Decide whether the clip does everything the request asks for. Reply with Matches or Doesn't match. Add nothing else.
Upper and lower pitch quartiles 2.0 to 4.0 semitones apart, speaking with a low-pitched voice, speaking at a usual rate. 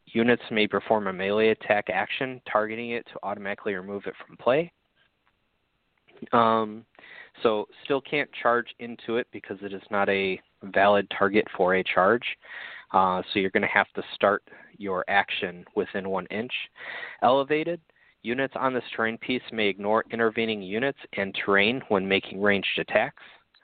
Matches